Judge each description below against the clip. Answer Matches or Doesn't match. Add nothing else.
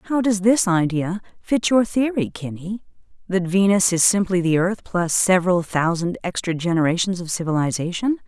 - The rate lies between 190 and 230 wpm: Doesn't match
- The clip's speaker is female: Matches